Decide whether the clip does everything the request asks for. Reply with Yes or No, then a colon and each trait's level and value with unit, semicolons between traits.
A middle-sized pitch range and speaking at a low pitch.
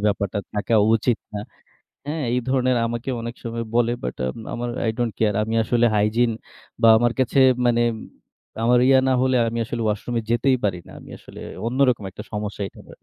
No: narrow, 2.3 semitones; low, 115 Hz